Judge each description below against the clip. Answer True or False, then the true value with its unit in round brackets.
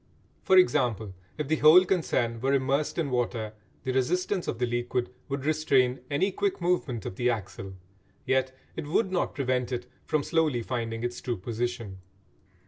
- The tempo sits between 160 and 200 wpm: True (165 wpm)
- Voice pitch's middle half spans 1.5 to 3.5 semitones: False (4.4 semitones)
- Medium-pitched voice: False (130 Hz)